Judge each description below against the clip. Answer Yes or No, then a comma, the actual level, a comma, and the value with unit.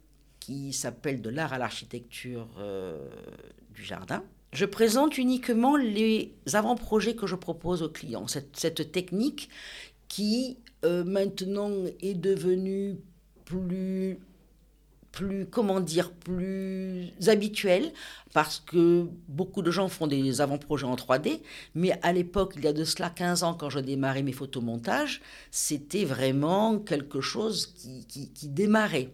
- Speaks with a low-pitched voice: No, medium, 175 Hz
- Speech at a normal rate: No, slow, 135 wpm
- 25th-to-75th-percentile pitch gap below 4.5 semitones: No, wide, 5.5 semitones